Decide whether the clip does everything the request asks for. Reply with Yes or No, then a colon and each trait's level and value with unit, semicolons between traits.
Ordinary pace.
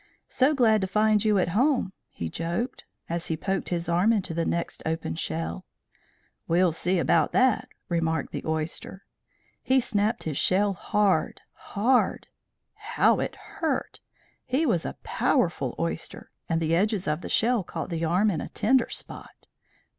Yes: average, 160 wpm